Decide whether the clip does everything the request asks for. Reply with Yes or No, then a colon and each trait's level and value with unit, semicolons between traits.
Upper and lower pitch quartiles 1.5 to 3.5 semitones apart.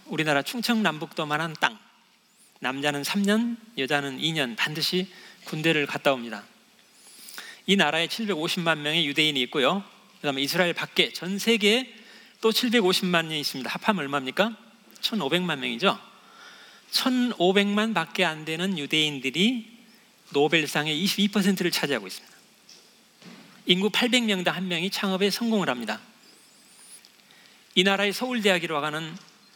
No: average, 5.3 semitones